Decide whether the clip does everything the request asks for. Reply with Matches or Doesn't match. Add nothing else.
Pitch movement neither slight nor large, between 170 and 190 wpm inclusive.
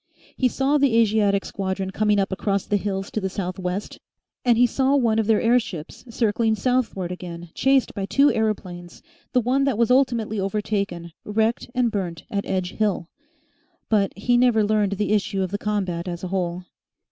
Matches